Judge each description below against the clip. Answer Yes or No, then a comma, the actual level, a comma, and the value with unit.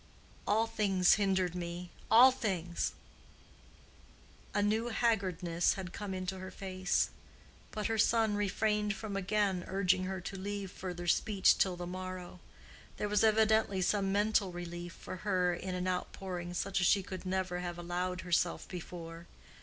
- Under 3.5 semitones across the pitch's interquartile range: Yes, narrow, 2.4 semitones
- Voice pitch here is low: No, medium, 185 Hz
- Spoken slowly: No, average, 145 wpm